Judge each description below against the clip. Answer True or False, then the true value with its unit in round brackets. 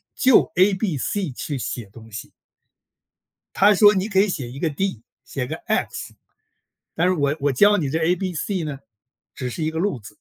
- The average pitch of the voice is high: False (165 Hz)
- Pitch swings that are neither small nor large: False (6.0 semitones)